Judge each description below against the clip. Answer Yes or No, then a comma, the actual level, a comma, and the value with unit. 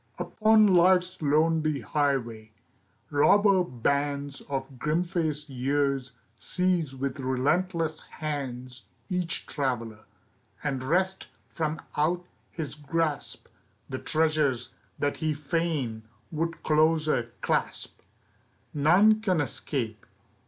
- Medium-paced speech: No, slow, 95 wpm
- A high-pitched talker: No, medium, 150 Hz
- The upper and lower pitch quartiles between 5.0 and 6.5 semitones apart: No, average, 3.8 semitones